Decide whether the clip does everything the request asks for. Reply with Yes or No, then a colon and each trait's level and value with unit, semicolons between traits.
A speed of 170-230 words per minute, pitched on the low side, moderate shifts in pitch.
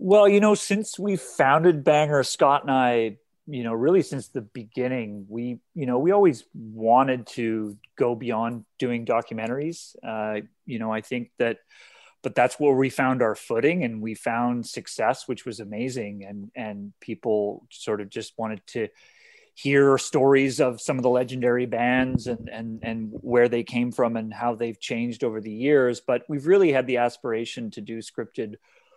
Yes: average, 180 wpm; low, 120 Hz; average, 3.2 semitones